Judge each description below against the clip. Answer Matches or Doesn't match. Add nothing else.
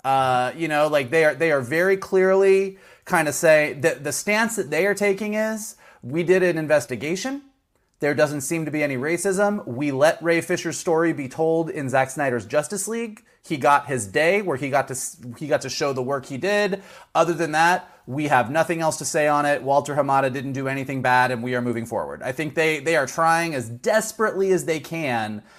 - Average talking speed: Doesn't match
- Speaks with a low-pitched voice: Doesn't match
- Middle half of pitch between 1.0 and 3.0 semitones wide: Doesn't match